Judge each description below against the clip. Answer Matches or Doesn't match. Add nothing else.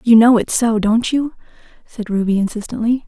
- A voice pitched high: Matches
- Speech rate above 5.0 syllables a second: Matches